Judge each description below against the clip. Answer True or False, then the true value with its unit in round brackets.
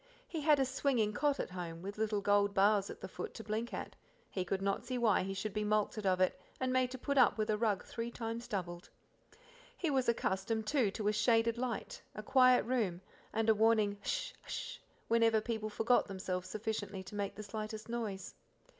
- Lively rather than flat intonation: False (2.9 semitones)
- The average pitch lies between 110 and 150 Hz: False (215 Hz)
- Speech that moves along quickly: True (210 wpm)